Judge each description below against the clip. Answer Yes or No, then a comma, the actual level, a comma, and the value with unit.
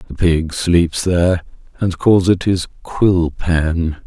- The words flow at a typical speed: Yes, average, 145 wpm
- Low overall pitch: Yes, very low, 85 Hz